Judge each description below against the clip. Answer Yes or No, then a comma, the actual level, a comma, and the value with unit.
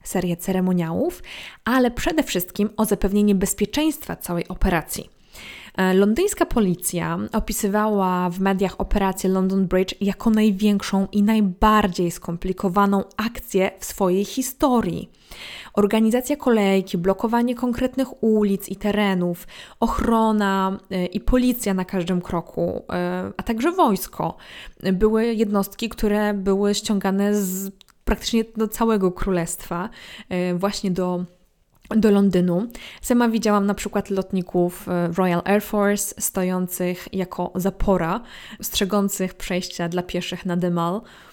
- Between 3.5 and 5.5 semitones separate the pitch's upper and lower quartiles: No, average, 2.9 semitones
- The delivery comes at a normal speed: No, slow, 105 wpm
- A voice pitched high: Yes, high, 195 Hz